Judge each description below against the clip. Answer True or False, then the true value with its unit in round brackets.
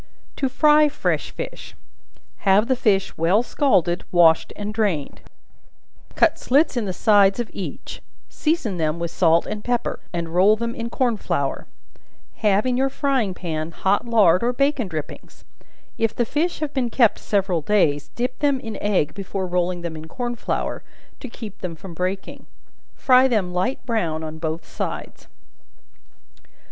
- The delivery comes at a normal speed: True (160 wpm)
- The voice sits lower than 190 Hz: False (205 Hz)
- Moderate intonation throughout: False (5.9 semitones)